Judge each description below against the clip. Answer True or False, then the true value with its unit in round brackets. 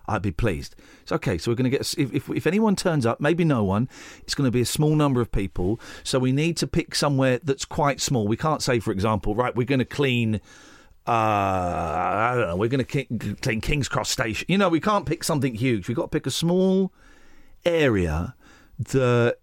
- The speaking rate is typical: False (230 wpm)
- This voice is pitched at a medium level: False (130 Hz)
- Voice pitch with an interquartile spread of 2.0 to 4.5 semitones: False (5.4 semitones)